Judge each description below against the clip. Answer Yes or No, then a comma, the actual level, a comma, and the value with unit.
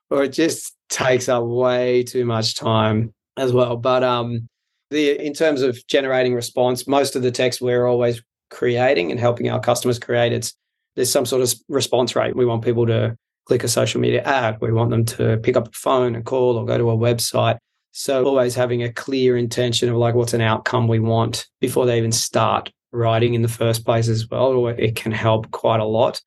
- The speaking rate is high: Yes, fast, 210 wpm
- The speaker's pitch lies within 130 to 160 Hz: No, low, 120 Hz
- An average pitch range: No, narrow, 1.6 semitones